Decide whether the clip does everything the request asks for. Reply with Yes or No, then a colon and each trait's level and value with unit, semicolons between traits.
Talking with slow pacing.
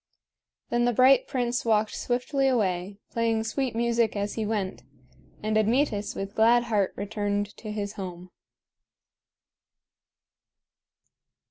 Yes: slow, 115 wpm